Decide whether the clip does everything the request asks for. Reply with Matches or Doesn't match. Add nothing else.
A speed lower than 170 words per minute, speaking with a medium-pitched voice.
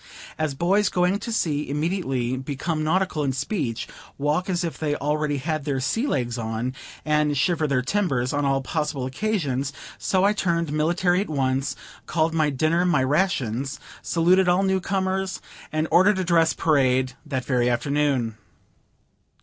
Matches